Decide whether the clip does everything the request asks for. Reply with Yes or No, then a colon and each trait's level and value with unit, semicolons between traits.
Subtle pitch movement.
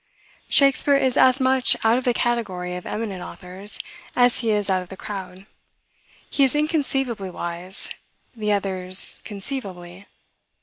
No: wide, 5.4 semitones